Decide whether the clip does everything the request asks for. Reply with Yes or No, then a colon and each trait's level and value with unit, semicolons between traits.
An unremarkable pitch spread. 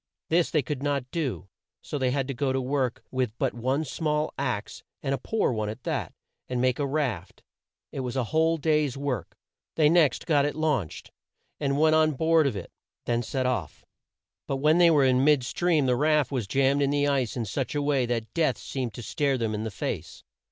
Yes: average, 3.5 semitones